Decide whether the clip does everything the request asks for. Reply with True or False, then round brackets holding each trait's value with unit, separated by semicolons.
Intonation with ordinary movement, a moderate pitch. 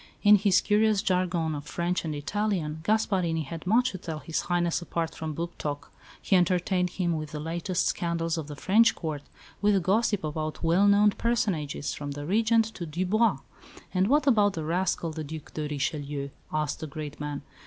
True (4.5 semitones; 170 Hz)